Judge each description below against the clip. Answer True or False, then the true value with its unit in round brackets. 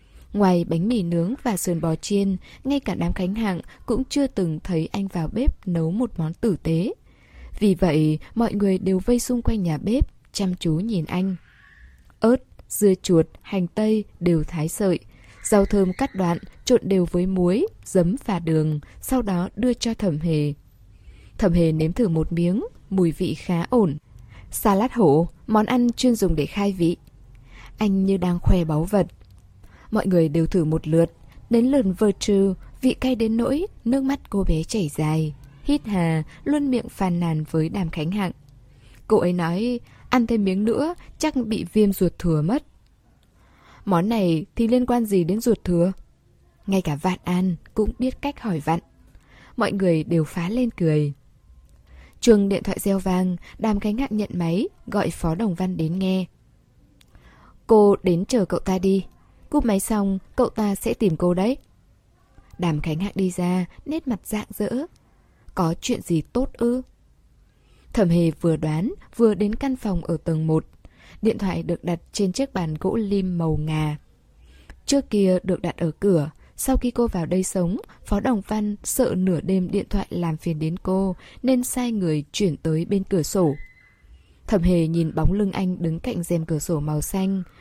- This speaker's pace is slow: False (185 wpm)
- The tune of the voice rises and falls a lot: False (4.7 semitones)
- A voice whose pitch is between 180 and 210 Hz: True (185 Hz)